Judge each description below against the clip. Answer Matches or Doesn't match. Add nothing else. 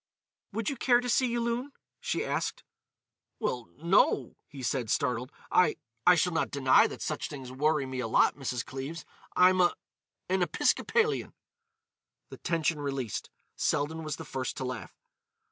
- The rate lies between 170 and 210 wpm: Doesn't match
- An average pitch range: Doesn't match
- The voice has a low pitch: Doesn't match